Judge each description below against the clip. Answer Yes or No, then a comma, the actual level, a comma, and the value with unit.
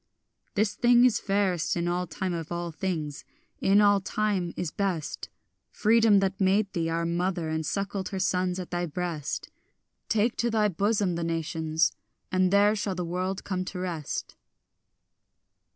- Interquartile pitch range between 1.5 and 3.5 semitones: Yes, average, 3.0 semitones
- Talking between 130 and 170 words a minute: Yes, average, 160 wpm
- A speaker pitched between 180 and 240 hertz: Yes, medium, 185 Hz